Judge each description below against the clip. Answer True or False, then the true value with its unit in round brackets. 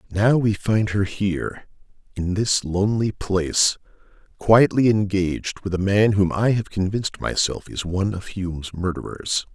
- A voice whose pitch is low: True (100 Hz)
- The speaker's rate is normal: True (150 wpm)